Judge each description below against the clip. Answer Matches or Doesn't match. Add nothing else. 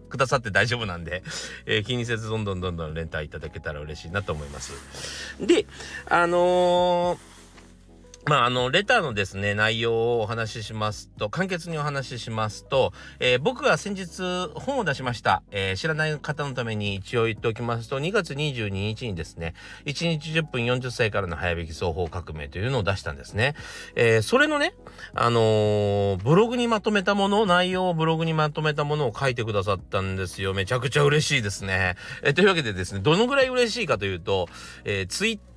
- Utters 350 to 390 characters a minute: Matches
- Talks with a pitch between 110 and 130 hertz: Matches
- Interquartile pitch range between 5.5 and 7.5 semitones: Doesn't match